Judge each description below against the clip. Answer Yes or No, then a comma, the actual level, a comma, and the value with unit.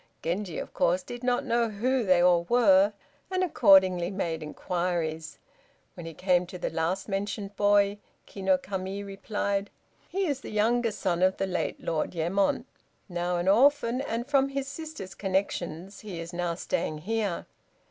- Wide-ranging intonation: No, average, 4.5 semitones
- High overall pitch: Yes, high, 195 Hz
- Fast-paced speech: No, average, 165 wpm